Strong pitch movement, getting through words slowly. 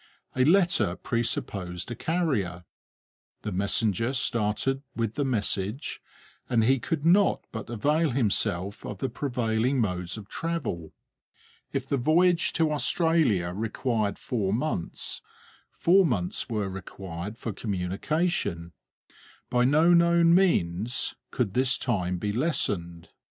Yes: wide, 7.4 semitones; slow, 120 wpm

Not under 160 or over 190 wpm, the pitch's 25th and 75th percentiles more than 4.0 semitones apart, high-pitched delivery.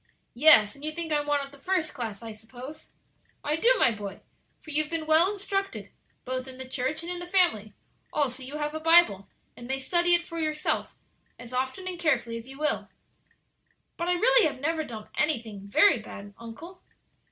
No: fast, 205 wpm; wide, 5.6 semitones; very high, 295 Hz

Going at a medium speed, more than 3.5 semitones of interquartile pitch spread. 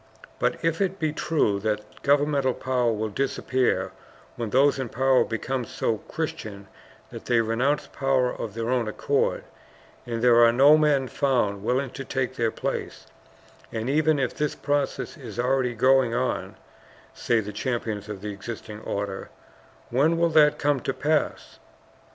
Yes: average, 155 wpm; average, 3.9 semitones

